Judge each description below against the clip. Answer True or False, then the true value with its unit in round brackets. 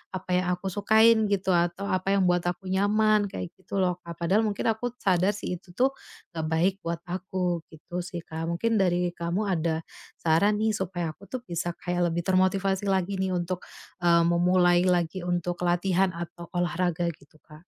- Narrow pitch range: True (2.1 semitones)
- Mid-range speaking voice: True (180 Hz)